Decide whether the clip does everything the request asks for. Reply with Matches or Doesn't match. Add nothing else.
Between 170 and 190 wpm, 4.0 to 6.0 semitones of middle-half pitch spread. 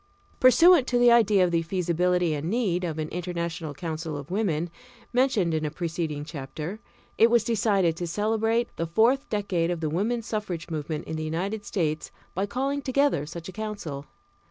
Matches